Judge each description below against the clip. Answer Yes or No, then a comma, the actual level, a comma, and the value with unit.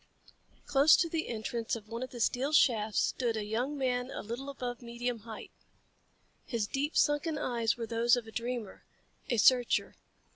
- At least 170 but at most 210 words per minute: Yes, average, 175 wpm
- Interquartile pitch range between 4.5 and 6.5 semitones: No, average, 2.7 semitones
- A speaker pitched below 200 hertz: No, high, 240 Hz